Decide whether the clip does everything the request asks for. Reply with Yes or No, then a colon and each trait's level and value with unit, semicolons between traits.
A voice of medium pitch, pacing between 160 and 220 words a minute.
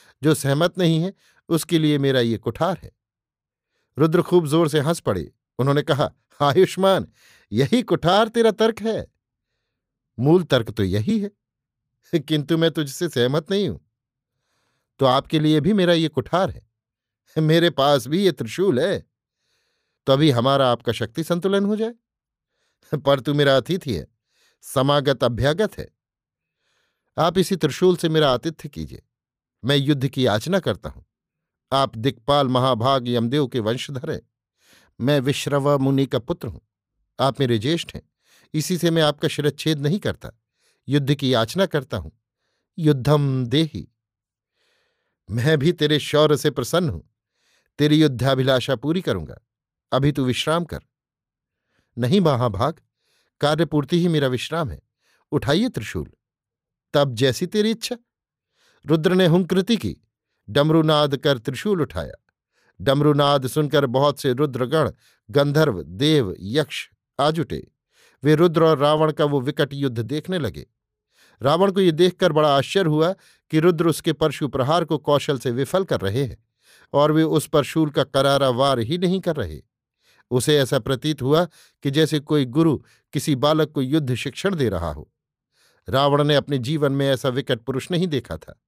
No: medium, 145 Hz; average, 150 wpm